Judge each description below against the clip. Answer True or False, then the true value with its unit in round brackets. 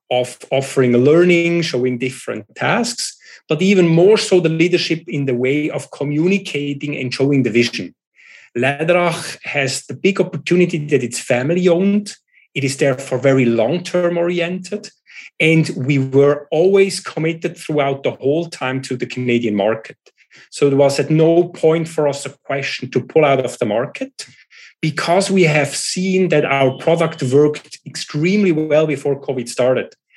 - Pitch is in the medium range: True (150 Hz)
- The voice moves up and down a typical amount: True (4.3 semitones)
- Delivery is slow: False (155 wpm)